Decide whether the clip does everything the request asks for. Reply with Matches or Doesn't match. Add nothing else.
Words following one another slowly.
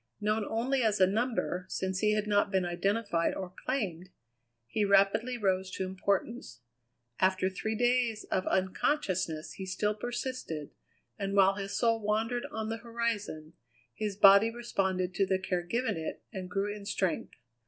Doesn't match